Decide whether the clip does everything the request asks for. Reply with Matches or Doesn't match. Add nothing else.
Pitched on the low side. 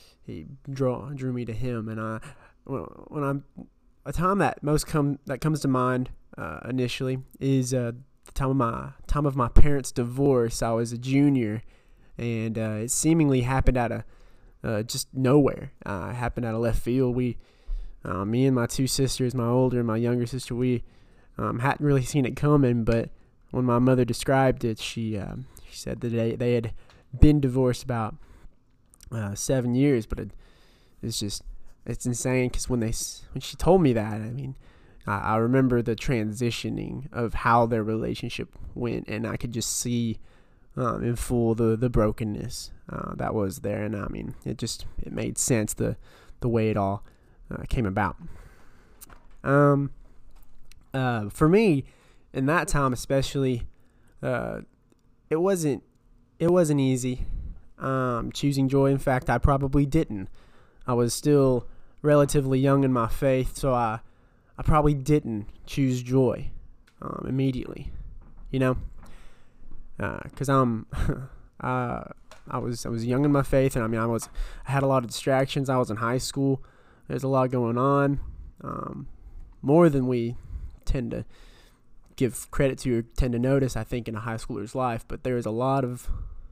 Matches